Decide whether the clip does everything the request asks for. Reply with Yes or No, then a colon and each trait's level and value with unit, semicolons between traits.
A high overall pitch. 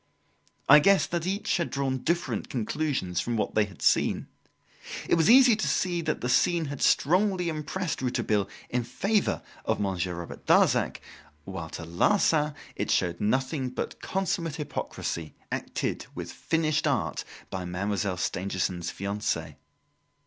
No: low, 135 Hz